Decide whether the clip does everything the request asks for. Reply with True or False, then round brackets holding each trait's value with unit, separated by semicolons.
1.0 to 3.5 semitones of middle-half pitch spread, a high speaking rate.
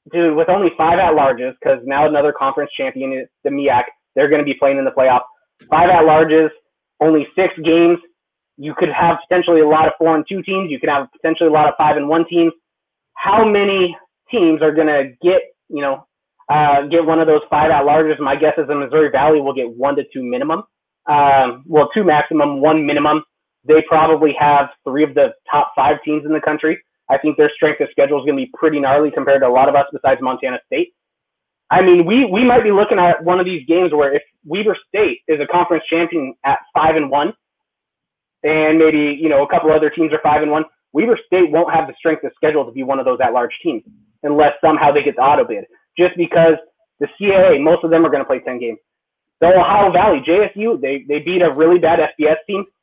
True (2.9 semitones; 225 wpm)